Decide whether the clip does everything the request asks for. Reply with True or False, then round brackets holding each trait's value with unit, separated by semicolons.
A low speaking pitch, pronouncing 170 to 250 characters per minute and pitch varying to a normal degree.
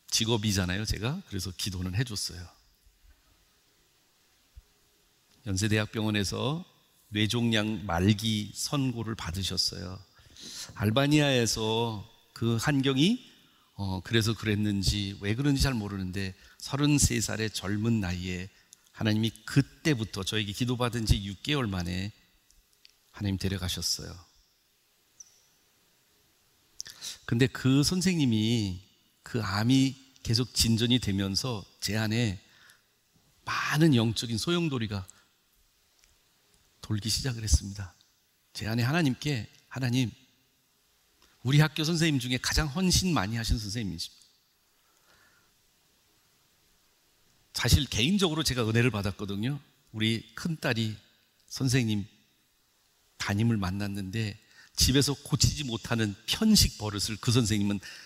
True (110 Hz; 235 characters per minute; 4.4 semitones)